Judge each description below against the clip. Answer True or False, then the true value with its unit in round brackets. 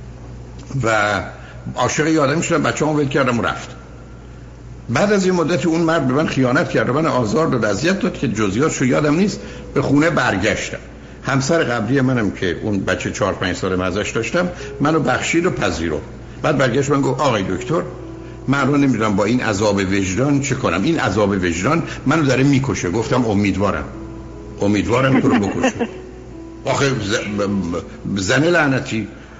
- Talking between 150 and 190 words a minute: True (155 wpm)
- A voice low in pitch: True (130 Hz)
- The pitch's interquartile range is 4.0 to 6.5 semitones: True (5.5 semitones)